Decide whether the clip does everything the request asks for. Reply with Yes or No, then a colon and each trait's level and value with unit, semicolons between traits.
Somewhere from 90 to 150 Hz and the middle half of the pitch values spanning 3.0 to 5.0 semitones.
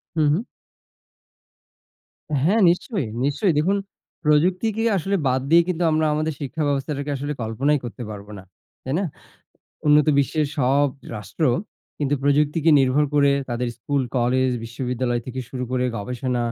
Yes: medium, 140 Hz; average, 3.6 semitones